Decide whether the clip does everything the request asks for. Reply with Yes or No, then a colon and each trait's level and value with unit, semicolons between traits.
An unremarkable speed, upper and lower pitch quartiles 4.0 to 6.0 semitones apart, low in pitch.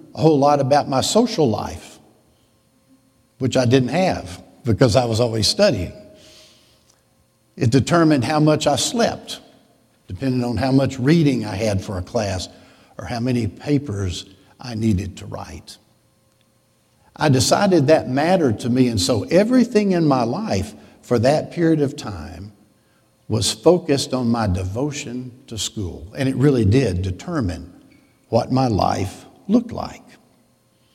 Yes: average, 145 wpm; average, 4.9 semitones; low, 125 Hz